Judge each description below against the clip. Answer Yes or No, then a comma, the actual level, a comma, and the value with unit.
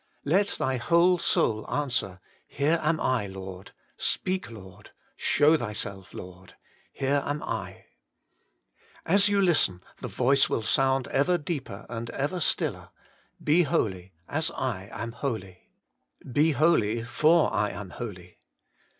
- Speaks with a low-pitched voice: Yes, low, 130 Hz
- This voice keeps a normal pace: No, slow, 130 wpm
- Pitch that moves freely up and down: Yes, wide, 7.6 semitones